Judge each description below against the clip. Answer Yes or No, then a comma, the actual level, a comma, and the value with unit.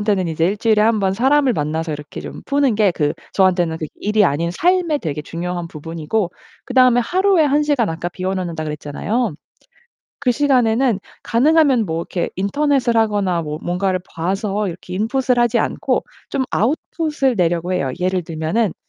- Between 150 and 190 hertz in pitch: No, high, 200 Hz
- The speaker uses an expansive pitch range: Yes, wide, 6.9 semitones